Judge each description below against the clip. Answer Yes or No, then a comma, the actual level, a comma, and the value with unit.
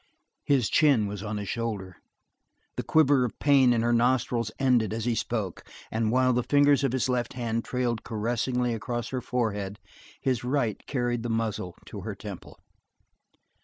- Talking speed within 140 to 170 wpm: Yes, average, 165 wpm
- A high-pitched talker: No, low, 120 Hz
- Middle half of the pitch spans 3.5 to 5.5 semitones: No, narrow, 2.6 semitones